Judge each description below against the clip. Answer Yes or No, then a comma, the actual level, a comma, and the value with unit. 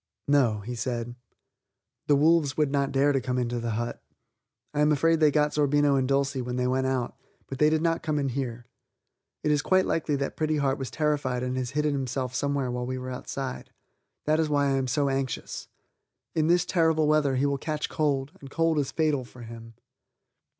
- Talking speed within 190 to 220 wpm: Yes, fast, 205 wpm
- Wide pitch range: No, average, 2.9 semitones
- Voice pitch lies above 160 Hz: No, medium, 140 Hz